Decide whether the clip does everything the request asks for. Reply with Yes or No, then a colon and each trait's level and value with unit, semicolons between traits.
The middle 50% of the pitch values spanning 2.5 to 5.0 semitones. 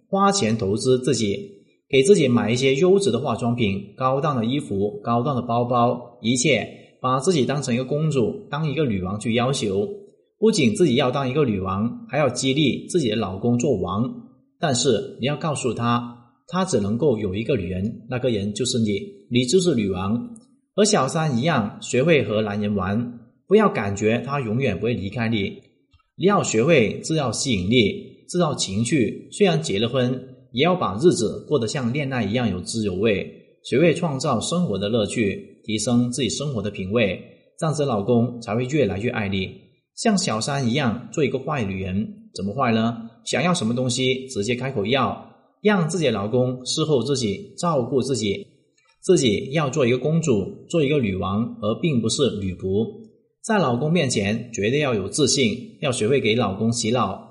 No: wide, 5.6 semitones